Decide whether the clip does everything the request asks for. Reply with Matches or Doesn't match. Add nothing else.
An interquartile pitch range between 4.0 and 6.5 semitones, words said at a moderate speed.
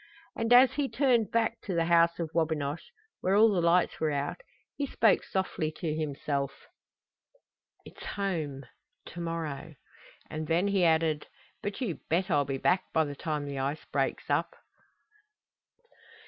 Matches